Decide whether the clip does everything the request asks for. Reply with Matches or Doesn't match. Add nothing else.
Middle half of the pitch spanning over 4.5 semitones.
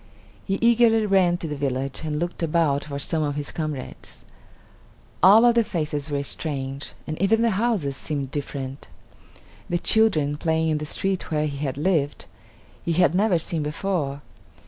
Matches